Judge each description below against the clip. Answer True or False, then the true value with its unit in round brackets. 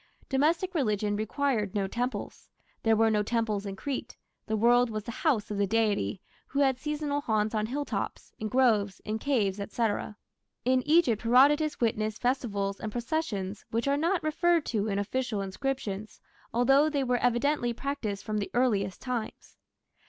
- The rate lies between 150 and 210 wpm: True (160 wpm)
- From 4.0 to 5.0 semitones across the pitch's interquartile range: True (4.7 semitones)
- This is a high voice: True (235 Hz)